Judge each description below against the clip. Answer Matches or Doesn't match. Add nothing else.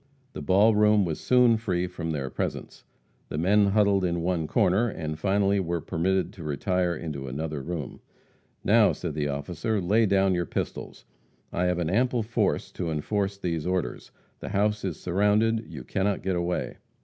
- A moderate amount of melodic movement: Matches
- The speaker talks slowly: Doesn't match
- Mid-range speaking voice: Doesn't match